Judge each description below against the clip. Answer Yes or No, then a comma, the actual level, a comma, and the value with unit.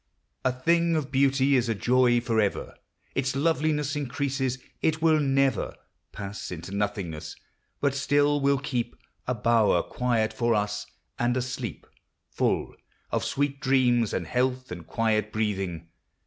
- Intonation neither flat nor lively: Yes, average, 4.4 semitones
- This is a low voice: Yes, low, 125 Hz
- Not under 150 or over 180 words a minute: No, average, 140 wpm